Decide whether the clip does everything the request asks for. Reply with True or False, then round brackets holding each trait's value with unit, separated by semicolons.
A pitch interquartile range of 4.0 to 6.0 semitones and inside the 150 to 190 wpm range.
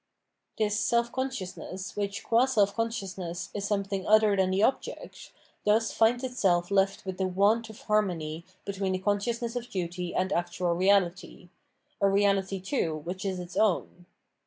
False (2.8 semitones; 155 wpm)